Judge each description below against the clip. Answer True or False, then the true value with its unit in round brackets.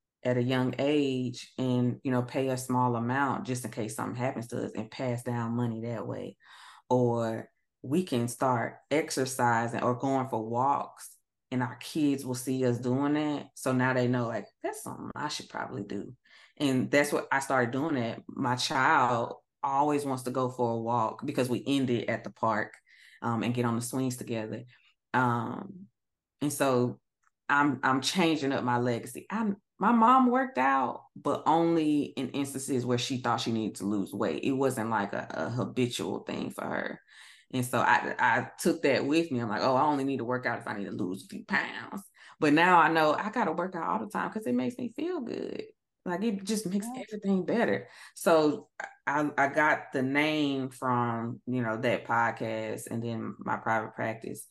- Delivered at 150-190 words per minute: False (200 wpm)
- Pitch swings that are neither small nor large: True (3.4 semitones)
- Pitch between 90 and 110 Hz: False (130 Hz)